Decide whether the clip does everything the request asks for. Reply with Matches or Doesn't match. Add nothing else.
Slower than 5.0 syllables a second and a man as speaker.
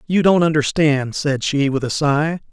Matches